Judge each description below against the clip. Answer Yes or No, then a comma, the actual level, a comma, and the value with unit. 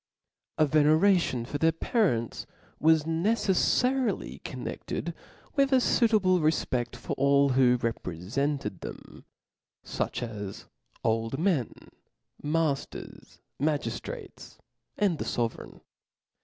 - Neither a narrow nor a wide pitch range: No, wide, 6.9 semitones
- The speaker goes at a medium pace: No, slow, 100 wpm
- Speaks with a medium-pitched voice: Yes, medium, 150 Hz